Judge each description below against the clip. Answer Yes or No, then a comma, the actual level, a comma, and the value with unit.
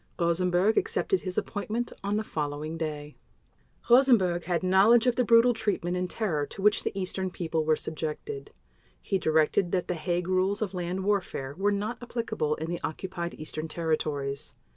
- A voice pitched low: No, medium, 180 Hz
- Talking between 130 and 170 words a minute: Yes, average, 165 wpm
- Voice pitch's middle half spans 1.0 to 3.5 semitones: No, average, 4.4 semitones